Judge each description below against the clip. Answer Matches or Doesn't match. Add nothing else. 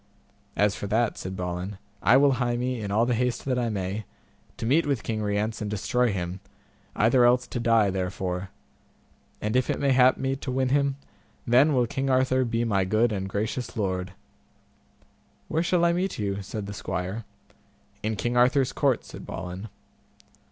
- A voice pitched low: Matches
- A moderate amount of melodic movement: Matches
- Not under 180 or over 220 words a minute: Matches